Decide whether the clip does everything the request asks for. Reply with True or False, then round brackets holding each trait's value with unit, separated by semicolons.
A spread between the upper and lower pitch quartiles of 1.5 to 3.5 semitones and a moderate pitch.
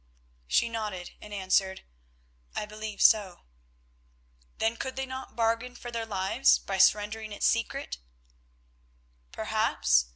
False (3.1 semitones; 215 Hz)